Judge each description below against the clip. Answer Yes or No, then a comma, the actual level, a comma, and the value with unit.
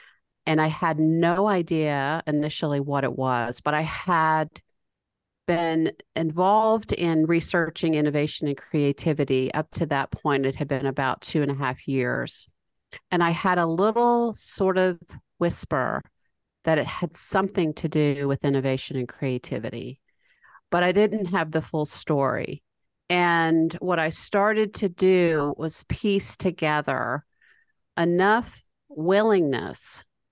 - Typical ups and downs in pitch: Yes, average, 4.1 semitones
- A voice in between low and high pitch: Yes, medium, 160 Hz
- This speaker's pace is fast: No, slow, 135 wpm